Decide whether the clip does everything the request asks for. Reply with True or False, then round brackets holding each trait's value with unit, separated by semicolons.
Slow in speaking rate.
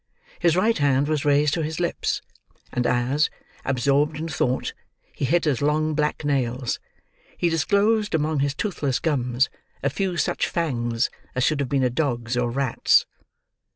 False (160 wpm)